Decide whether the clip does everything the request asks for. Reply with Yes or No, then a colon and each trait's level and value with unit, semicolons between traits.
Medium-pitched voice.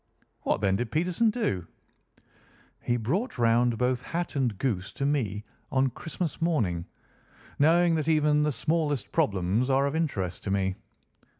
No: low, 130 Hz